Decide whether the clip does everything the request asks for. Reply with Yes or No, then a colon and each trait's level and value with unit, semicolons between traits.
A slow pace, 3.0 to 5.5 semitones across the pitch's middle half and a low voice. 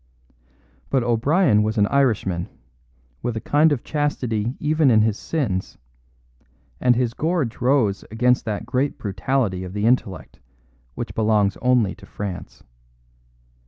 Yes: slow, 130 wpm; average, 4.6 semitones; low, 115 Hz